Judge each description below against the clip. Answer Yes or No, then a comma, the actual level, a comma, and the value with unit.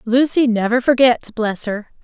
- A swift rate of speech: No, average, 150 wpm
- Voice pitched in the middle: No, high, 235 Hz